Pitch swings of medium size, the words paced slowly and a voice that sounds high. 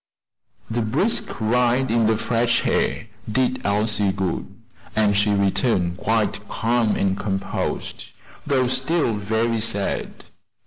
No: average, 3.0 semitones; slow, 120 wpm; low, 110 Hz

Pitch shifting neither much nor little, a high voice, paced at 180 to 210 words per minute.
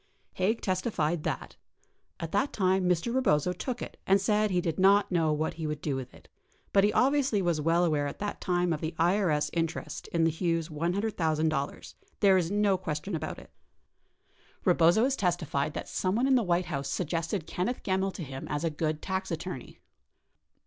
No: average, 3.8 semitones; medium, 175 Hz; average, 190 wpm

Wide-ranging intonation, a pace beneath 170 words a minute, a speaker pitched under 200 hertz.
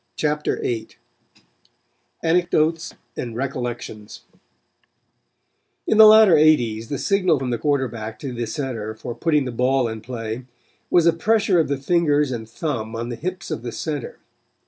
Yes: wide, 5.7 semitones; average, 150 wpm; low, 135 Hz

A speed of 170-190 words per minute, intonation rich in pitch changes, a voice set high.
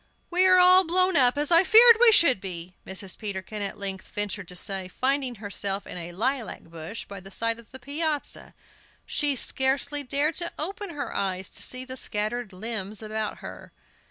Yes: average, 185 wpm; wide, 7.0 semitones; high, 240 Hz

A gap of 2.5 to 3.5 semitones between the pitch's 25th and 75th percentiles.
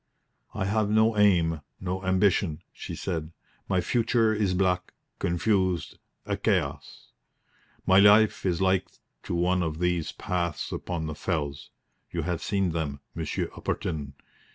Yes: average, 3.1 semitones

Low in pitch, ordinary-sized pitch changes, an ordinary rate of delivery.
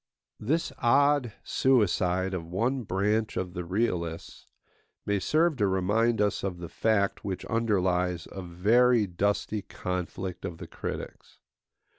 No: low, 100 Hz; average, 4.1 semitones; slow, 130 wpm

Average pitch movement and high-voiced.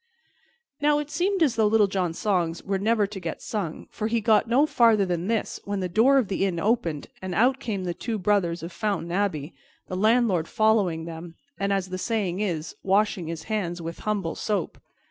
Yes: average, 4.1 semitones; high, 200 Hz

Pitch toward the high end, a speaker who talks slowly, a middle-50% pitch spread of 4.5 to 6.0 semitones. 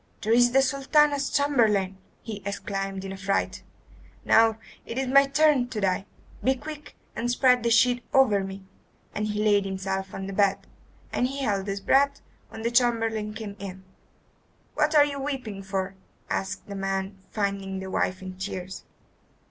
No: high, 210 Hz; average, 165 wpm; average, 5.0 semitones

